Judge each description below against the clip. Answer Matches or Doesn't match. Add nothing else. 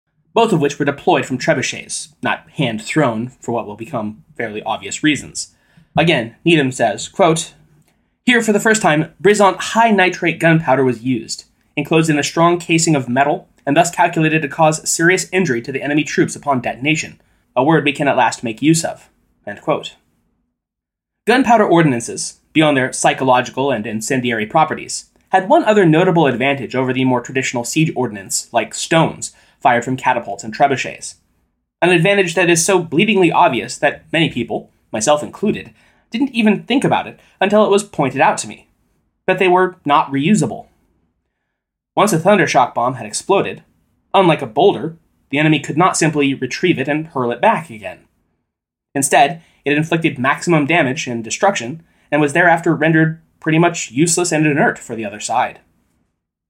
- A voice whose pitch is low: Doesn't match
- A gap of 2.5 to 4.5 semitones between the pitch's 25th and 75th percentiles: Doesn't match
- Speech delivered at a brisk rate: Doesn't match